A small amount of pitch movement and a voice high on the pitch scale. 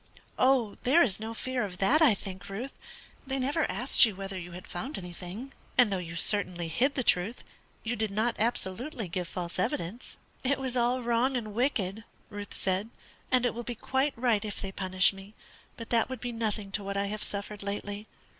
No: average, 4.2 semitones; high, 215 Hz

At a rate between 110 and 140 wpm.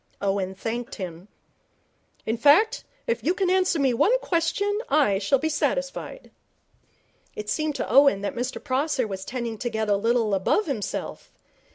No: average, 160 wpm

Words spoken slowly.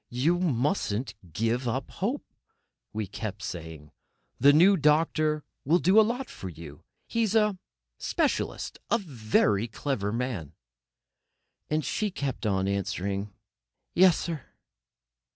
Yes: slow, 120 wpm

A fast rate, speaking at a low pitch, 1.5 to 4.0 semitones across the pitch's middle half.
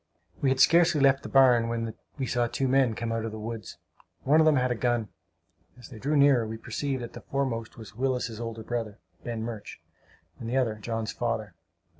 Yes: fast, 210 wpm; low, 120 Hz; average, 2.9 semitones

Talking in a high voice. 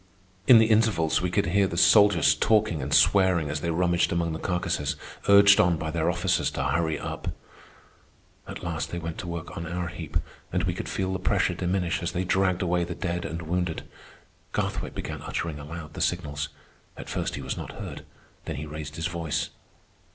No: very low, 85 Hz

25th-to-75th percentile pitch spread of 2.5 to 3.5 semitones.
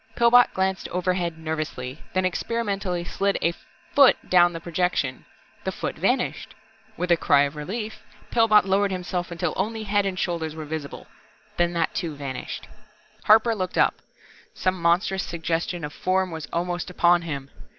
Yes: average, 2.9 semitones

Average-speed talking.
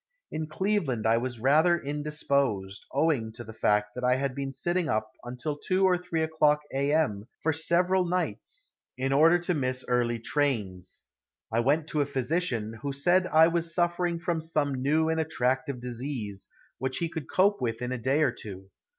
Yes: average, 185 wpm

